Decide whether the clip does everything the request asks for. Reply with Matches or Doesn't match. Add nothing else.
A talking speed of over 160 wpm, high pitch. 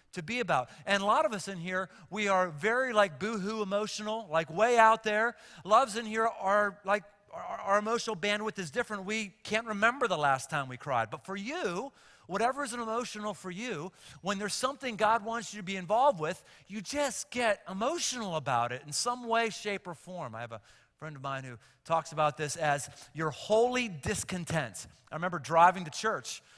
Matches